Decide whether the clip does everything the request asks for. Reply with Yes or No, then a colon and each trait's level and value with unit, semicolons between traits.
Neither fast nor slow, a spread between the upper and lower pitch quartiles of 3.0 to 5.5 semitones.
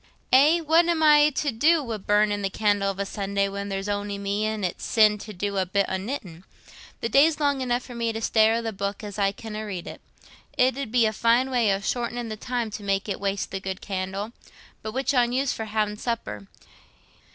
No: fast, 220 wpm; average, 3.6 semitones